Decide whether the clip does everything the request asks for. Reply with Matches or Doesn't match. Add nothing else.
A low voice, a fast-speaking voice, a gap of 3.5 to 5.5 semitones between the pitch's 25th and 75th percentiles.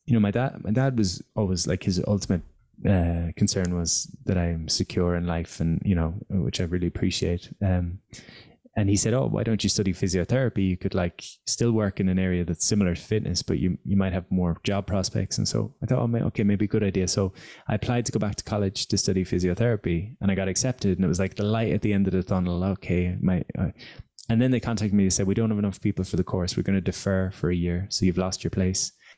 Doesn't match